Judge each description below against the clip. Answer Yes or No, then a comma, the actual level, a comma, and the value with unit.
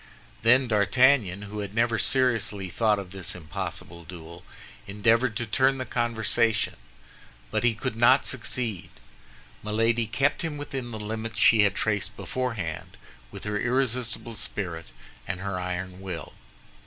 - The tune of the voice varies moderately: Yes, average, 3.6 semitones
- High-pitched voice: No, low, 110 Hz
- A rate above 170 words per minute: No, average, 140 wpm